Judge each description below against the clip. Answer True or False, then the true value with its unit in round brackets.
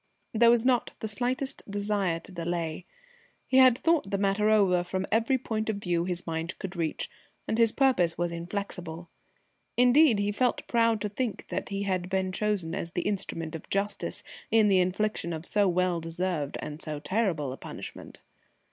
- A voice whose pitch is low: False (195 Hz)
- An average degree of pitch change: True (4.2 semitones)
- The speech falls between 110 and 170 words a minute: False (180 wpm)